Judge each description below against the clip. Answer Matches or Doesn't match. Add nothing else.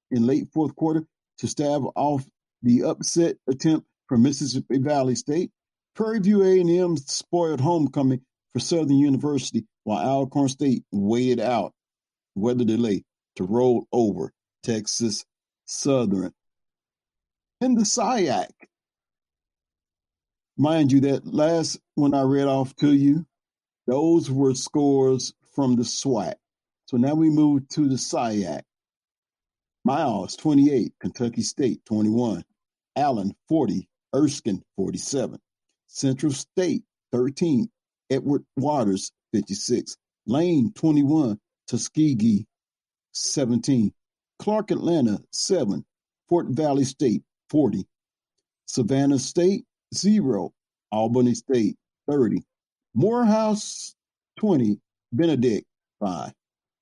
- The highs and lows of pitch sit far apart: Doesn't match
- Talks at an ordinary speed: Doesn't match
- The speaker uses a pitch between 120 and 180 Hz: Matches